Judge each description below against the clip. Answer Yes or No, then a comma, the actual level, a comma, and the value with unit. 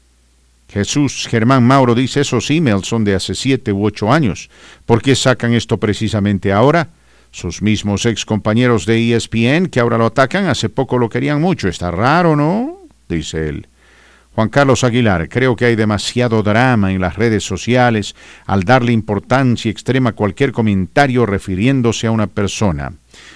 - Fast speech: No, average, 160 wpm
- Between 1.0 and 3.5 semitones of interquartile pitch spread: No, average, 4.2 semitones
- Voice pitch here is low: Yes, low, 115 Hz